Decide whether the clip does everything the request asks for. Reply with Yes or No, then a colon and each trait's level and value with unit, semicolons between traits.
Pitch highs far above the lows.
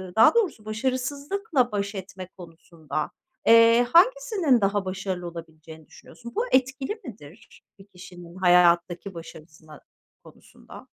Yes: wide, 7.0 semitones